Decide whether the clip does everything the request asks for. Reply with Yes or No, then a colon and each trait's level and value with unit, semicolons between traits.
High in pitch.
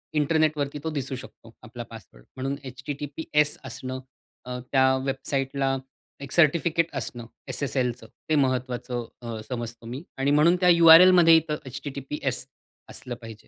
No: low, 135 Hz